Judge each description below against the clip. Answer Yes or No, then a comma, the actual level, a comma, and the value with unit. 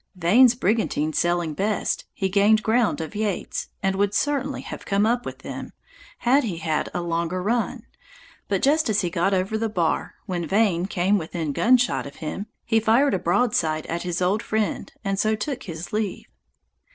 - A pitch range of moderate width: Yes, average, 4.3 semitones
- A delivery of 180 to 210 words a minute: Yes, average, 190 wpm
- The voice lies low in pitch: No, high, 200 Hz